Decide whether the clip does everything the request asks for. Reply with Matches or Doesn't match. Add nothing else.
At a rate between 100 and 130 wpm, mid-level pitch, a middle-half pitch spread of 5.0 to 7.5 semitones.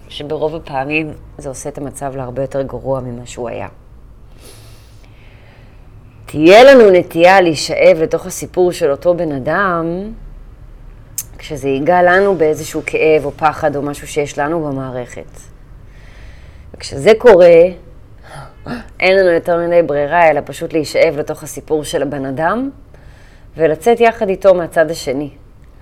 Matches